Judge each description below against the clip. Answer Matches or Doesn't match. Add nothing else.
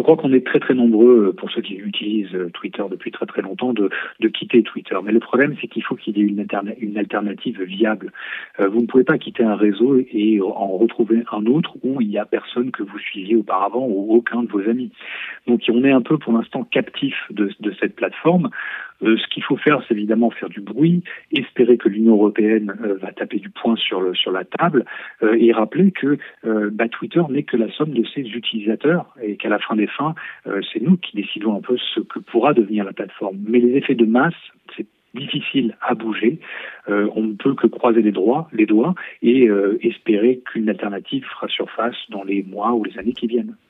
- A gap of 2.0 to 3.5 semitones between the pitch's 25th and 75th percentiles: Matches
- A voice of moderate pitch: Doesn't match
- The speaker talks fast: Matches